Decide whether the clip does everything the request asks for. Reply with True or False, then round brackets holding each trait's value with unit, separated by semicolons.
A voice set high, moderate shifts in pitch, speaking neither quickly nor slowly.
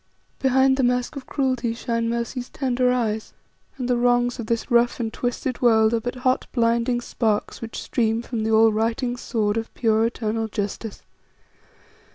False (235 Hz; 1.8 semitones; 170 wpm)